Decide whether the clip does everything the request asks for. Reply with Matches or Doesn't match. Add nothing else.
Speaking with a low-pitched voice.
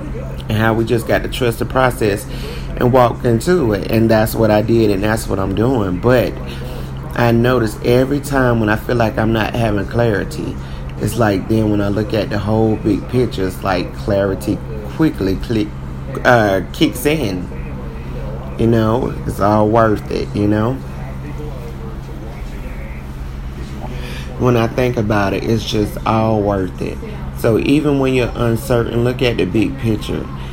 Matches